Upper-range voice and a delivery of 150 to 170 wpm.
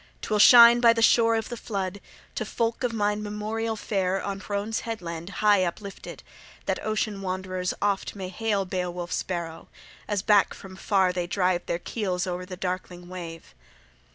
Yes: high, 195 Hz; average, 165 wpm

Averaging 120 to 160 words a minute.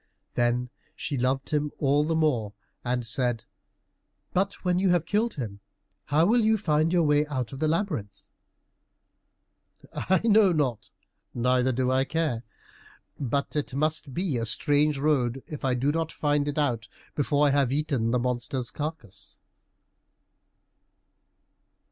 Yes: average, 150 wpm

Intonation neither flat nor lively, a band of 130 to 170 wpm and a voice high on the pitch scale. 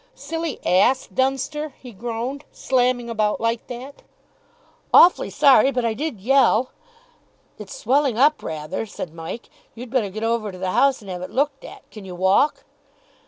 Yes: average, 4.5 semitones; average, 165 wpm; high, 245 Hz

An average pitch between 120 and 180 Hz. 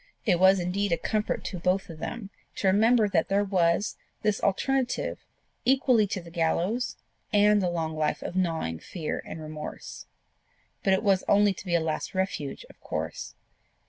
No: high, 190 Hz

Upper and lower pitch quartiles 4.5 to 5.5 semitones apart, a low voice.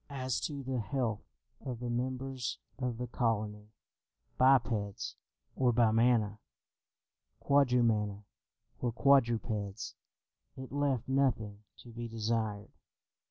No: average, 3.0 semitones; low, 120 Hz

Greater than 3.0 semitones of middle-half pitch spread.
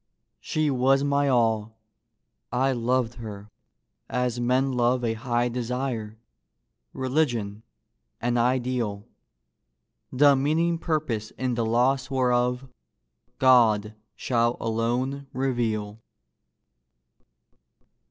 No: narrow, 2.6 semitones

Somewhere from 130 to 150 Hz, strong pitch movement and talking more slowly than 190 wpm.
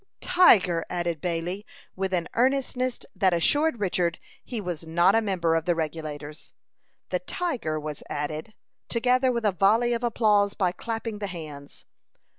No: high, 190 Hz; wide, 5.8 semitones; average, 150 wpm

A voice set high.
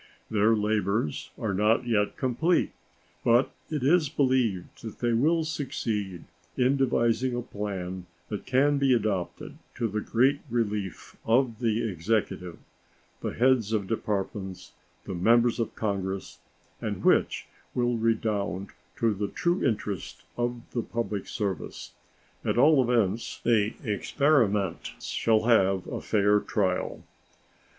No: low, 110 Hz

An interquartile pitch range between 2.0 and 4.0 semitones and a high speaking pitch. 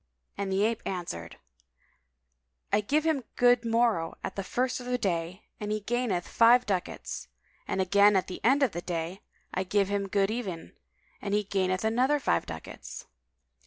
No: average, 4.4 semitones; high, 200 Hz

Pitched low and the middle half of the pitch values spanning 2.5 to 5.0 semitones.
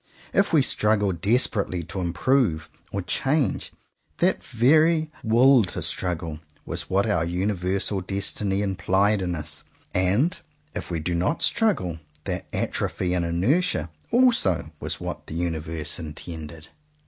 No: very low, 95 Hz; wide, 5.6 semitones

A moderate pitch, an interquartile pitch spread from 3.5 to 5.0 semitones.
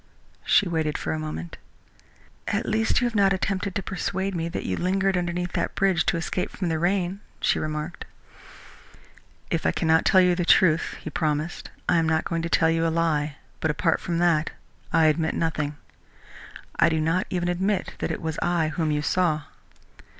No: medium, 165 Hz; narrow, 2.5 semitones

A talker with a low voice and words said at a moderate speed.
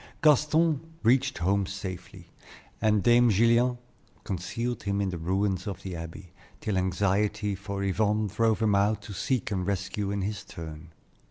Yes: low, 100 Hz; average, 155 wpm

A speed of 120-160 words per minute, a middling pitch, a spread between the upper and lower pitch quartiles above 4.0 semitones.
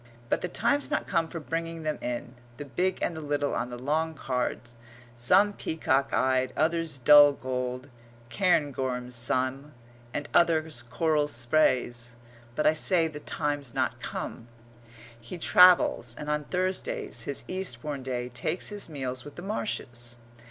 Yes: average, 150 wpm; medium, 145 Hz; average, 4.8 semitones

